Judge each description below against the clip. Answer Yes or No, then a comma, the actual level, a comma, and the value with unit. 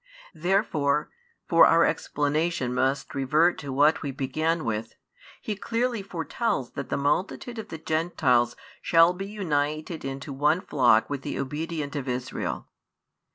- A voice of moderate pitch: Yes, medium, 150 Hz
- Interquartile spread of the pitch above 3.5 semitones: Yes, average, 4.0 semitones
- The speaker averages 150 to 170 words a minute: No, average, 140 wpm